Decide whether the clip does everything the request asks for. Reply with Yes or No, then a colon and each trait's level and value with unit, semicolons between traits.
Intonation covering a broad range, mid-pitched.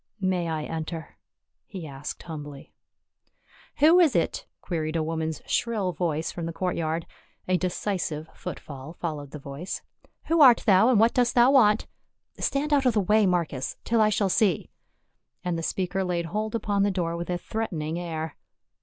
No: average, 4.9 semitones; medium, 180 Hz